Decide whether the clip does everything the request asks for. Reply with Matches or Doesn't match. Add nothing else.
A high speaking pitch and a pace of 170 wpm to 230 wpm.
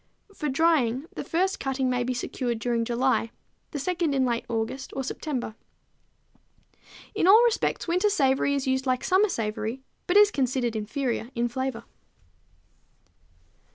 Doesn't match